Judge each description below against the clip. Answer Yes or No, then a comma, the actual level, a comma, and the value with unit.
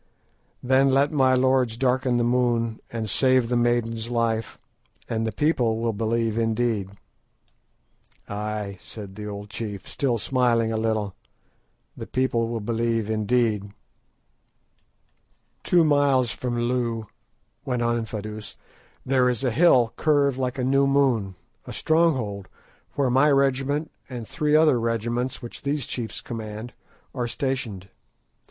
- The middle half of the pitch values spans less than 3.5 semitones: Yes, average, 2.9 semitones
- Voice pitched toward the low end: Yes, low, 120 Hz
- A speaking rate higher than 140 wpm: No, slow, 135 wpm